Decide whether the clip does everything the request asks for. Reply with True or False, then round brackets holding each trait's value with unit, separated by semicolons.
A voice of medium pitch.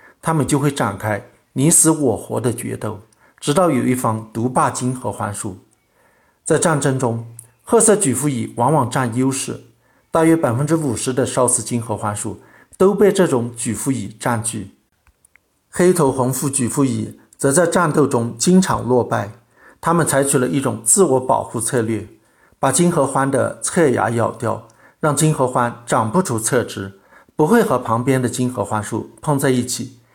False (125 Hz)